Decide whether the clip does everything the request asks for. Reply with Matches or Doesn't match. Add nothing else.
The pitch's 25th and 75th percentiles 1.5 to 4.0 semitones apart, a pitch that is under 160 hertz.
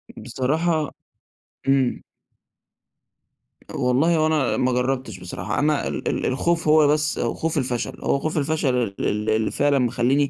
Matches